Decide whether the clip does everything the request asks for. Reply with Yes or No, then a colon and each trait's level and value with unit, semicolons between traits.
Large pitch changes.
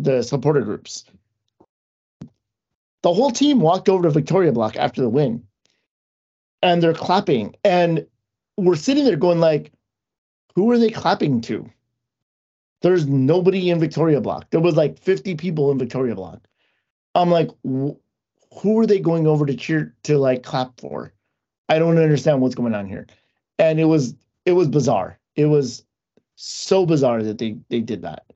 Yes: wide, 5.7 semitones